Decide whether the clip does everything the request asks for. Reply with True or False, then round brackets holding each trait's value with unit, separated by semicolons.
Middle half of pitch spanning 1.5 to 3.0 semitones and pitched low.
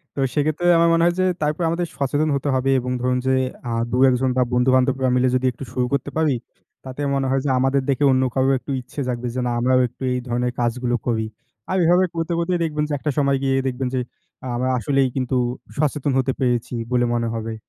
True (2.7 semitones; 130 Hz)